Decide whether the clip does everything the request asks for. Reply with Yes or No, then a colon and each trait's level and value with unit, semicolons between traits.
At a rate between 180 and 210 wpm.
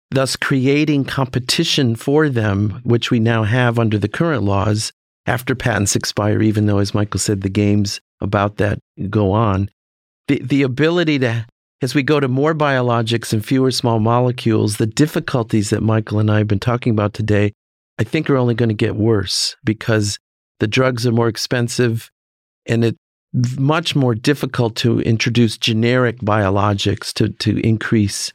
No: average, 165 wpm